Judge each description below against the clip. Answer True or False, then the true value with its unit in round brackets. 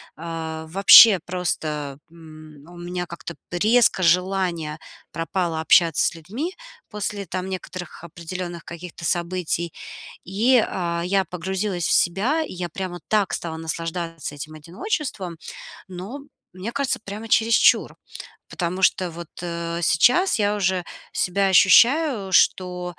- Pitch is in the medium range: True (180 Hz)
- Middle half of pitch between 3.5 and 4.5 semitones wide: False (2.8 semitones)